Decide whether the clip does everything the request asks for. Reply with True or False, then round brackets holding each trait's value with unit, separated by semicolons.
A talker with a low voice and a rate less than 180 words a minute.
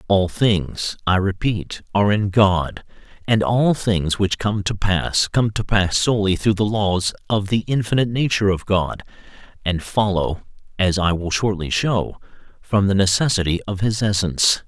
True (100 Hz; 165 wpm)